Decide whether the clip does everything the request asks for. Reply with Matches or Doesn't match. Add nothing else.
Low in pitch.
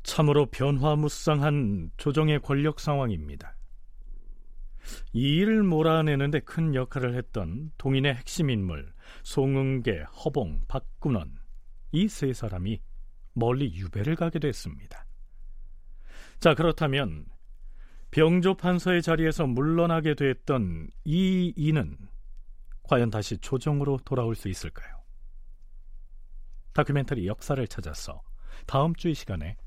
Matches